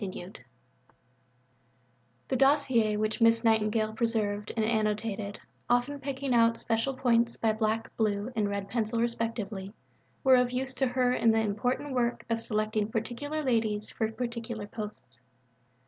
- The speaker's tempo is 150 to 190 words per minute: No, average, 140 wpm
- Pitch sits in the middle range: No, high, 225 Hz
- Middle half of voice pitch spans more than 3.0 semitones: No, narrow, 2.5 semitones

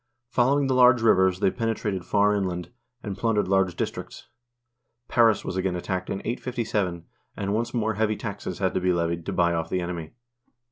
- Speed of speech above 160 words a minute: Yes, average, 180 wpm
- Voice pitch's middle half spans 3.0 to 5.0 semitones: Yes, average, 3.8 semitones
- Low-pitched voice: Yes, low, 100 Hz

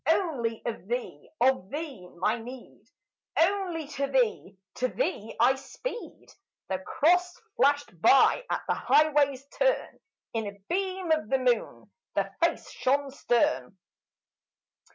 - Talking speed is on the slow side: Yes, slow, 130 wpm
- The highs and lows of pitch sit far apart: Yes, wide, 5.8 semitones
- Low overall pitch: No, very high, 270 Hz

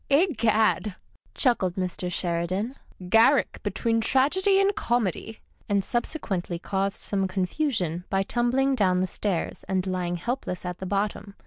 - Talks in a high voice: Yes, high, 200 Hz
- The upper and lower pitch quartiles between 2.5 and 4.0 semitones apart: No, average, 4.7 semitones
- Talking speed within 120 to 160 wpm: Yes, average, 150 wpm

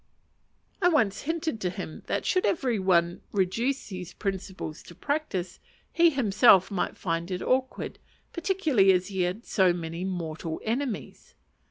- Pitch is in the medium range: No, high, 195 Hz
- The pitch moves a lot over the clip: Yes, wide, 6.5 semitones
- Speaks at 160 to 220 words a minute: No, average, 145 wpm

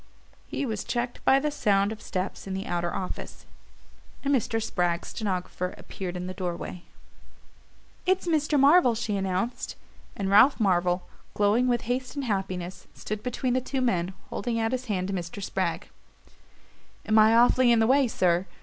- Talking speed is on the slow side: No, average, 170 wpm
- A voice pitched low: No, high, 215 Hz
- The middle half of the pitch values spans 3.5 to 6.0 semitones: Yes, average, 5.2 semitones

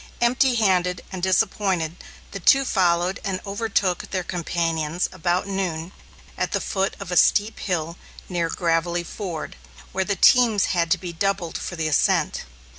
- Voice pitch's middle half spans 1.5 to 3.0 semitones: Yes, narrow, 2.6 semitones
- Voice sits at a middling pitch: Yes, medium, 180 Hz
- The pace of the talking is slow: No, average, 155 wpm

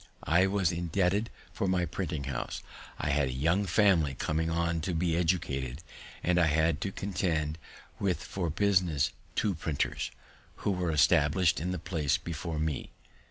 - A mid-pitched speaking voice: No, very low, 85 Hz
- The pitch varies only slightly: No, average, 3.0 semitones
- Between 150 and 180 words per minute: Yes, average, 160 wpm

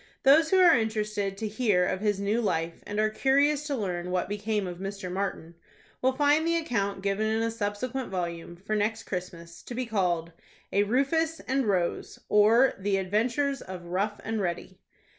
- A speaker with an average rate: Yes, average, 180 wpm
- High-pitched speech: Yes, high, 210 Hz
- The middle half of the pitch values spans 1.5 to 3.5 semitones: No, average, 5.0 semitones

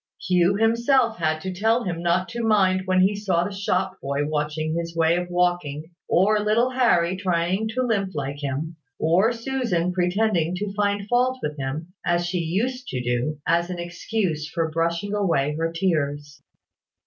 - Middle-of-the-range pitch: Yes, medium, 180 Hz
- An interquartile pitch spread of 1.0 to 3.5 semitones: No, average, 4.2 semitones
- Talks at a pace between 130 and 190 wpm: Yes, average, 170 wpm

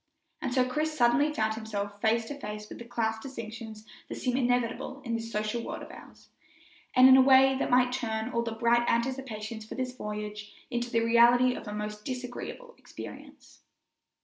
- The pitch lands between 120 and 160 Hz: No, high, 235 Hz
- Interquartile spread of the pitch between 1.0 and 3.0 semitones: Yes, narrow, 2.6 semitones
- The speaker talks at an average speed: Yes, average, 185 wpm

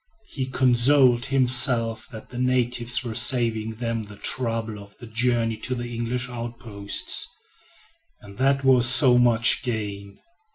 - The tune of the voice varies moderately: No, narrow, 2.1 semitones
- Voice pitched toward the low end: Yes, low, 120 Hz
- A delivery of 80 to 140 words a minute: Yes, slow, 135 wpm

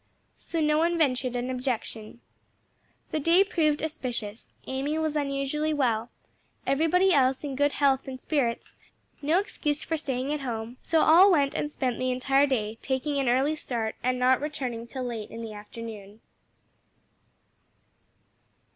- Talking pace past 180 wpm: No, average, 150 wpm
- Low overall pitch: No, very high, 270 Hz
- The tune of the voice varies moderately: Yes, average, 3.7 semitones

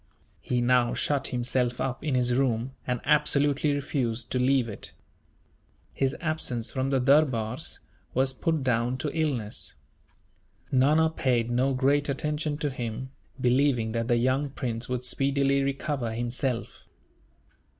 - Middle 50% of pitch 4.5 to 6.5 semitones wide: No, narrow, 2.5 semitones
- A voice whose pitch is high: No, low, 130 Hz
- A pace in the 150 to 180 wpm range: No, slow, 135 wpm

